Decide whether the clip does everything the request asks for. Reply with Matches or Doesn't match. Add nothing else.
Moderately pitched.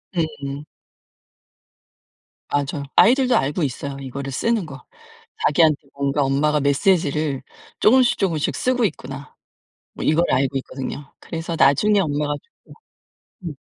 Matches